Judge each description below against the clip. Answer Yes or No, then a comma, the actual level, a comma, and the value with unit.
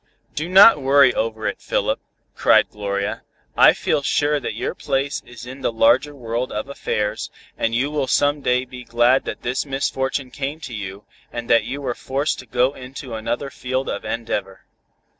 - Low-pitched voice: Yes, low, 130 Hz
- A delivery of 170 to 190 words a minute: Yes, average, 180 wpm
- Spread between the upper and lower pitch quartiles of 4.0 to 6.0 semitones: No, average, 3.2 semitones